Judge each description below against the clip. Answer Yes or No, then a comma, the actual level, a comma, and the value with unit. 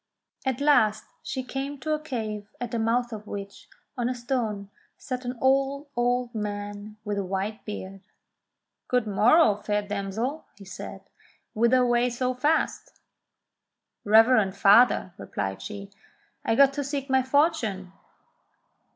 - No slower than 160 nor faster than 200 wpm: No, average, 140 wpm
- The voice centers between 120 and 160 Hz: No, high, 235 Hz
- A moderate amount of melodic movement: Yes, average, 4.1 semitones